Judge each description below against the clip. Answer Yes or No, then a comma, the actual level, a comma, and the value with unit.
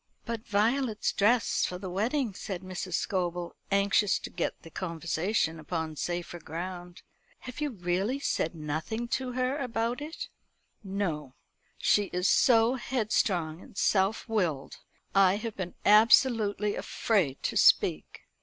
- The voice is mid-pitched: No, high, 200 Hz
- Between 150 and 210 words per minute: No, slow, 135 wpm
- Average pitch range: Yes, average, 4.6 semitones